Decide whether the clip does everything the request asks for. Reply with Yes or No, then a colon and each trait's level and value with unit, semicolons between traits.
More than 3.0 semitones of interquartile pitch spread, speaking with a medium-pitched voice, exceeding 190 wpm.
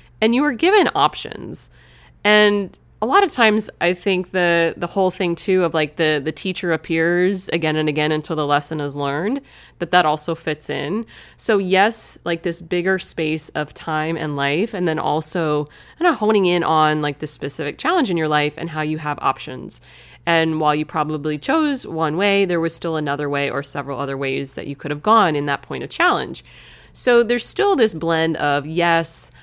Yes: average, 4.0 semitones; medium, 165 Hz; fast, 205 wpm